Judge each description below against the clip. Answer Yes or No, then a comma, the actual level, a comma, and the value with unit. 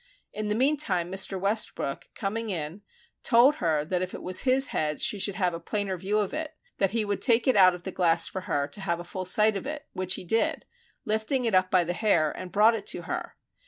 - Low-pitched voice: No, high, 195 Hz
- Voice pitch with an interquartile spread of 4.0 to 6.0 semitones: No, average, 3.6 semitones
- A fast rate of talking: Yes, fast, 245 wpm